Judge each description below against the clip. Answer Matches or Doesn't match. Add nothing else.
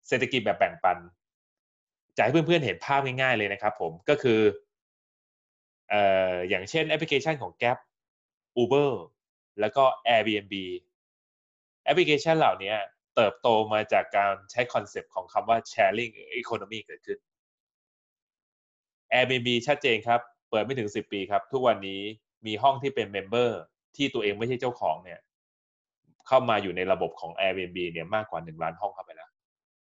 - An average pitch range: Doesn't match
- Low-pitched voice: Matches